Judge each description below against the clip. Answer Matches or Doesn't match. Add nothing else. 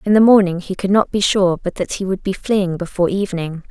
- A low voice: Doesn't match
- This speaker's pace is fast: Matches